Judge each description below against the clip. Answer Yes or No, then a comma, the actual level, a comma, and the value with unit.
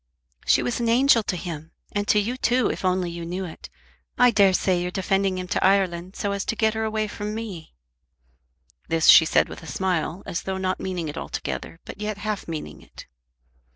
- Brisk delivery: Yes, fast, 210 wpm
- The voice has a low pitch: No, high, 190 Hz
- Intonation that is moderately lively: Yes, average, 3.4 semitones